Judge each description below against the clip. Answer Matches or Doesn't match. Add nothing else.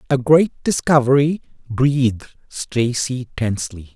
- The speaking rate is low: Matches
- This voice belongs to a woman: Doesn't match